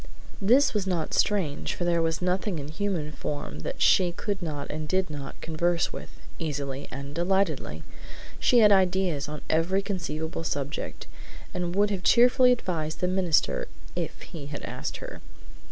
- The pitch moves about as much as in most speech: Yes, average, 4.1 semitones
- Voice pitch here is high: No, medium, 170 Hz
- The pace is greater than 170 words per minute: No, average, 160 wpm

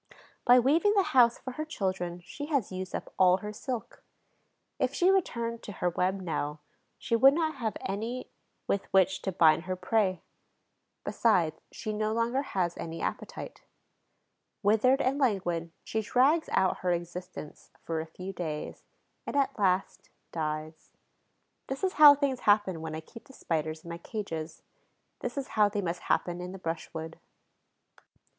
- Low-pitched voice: No, high, 195 Hz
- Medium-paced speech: Yes, average, 165 wpm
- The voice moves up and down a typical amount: No, wide, 6.3 semitones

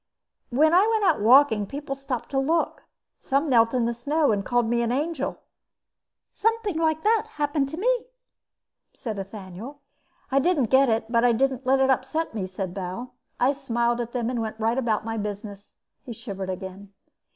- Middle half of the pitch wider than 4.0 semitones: Yes, average, 4.6 semitones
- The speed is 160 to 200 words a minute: Yes, average, 180 wpm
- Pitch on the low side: No, high, 245 Hz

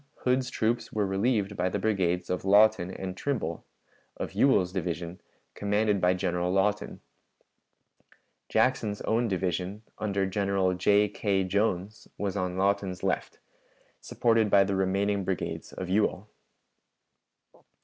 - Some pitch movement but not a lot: No, narrow, 2.2 semitones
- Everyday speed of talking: No, slow, 125 wpm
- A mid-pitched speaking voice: No, low, 100 Hz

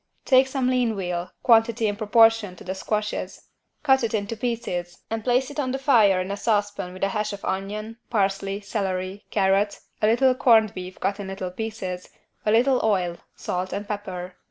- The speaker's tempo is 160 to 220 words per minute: Yes, average, 185 wpm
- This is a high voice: Yes, high, 210 Hz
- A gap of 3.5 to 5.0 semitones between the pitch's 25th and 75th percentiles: No, average, 3.1 semitones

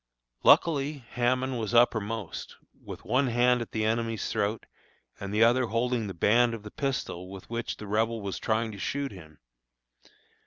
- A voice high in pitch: No, low, 115 Hz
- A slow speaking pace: No, average, 165 wpm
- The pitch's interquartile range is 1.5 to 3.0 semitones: Yes, average, 2.7 semitones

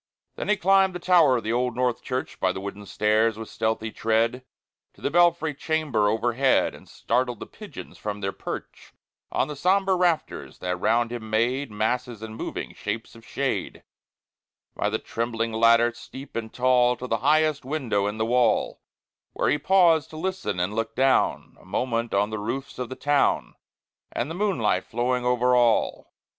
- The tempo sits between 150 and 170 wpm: No, average, 180 wpm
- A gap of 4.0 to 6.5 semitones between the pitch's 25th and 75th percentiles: Yes, average, 4.3 semitones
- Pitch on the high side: No, low, 120 Hz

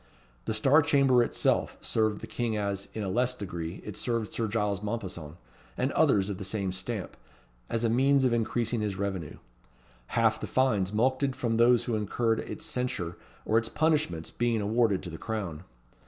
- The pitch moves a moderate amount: Yes, average, 3.4 semitones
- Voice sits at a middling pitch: No, low, 110 Hz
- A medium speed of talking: Yes, average, 180 wpm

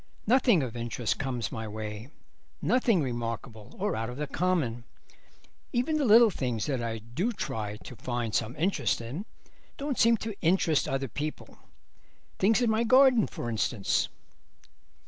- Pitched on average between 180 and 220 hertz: No, low, 135 Hz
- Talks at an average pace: Yes, average, 150 wpm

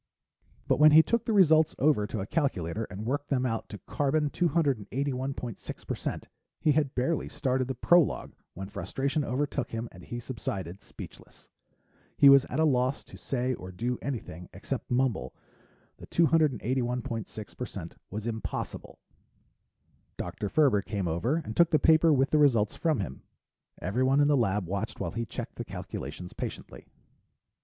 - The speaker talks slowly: No, average, 155 wpm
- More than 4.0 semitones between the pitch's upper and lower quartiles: Yes, wide, 5.4 semitones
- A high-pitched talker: No, low, 130 Hz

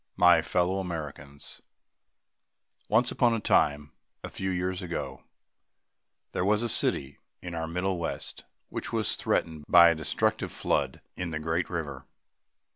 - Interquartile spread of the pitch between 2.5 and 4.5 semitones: Yes, average, 3.0 semitones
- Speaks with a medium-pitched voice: No, very low, 85 Hz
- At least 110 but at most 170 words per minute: Yes, average, 140 wpm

